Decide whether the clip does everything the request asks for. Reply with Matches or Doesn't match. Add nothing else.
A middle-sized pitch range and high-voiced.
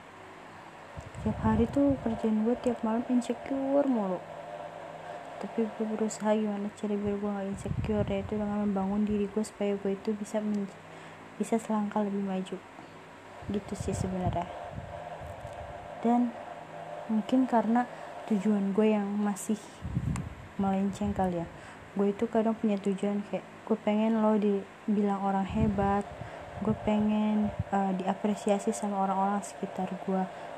Doesn't match